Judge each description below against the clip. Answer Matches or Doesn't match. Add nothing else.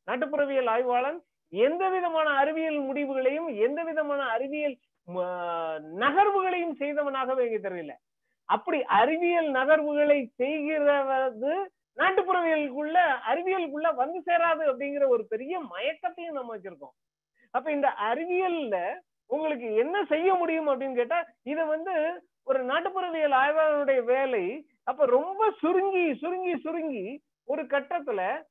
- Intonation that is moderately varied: Matches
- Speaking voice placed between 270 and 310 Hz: Matches